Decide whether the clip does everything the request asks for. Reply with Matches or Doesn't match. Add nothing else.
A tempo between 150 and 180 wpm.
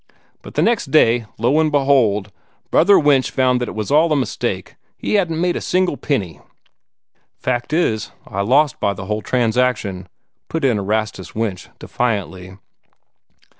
Matches